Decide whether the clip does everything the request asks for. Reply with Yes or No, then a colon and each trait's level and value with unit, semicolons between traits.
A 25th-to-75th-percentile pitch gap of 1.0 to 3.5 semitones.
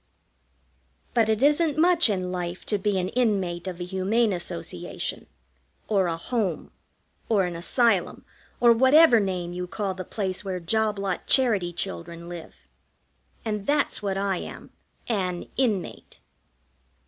No: average, 4.1 semitones